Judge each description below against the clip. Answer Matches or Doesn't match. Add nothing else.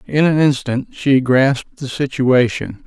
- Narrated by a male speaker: Matches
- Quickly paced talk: Doesn't match